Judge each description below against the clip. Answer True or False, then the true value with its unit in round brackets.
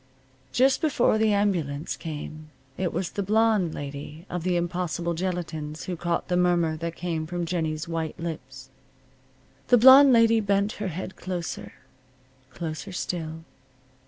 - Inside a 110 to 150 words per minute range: True (140 wpm)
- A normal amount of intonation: True (3.8 semitones)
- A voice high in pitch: False (175 Hz)